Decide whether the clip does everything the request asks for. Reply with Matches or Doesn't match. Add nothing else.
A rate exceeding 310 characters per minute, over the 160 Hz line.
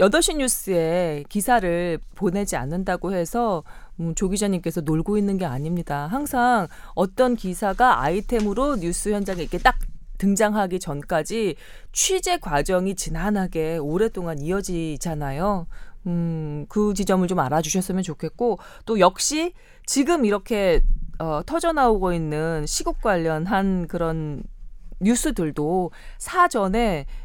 Doesn't match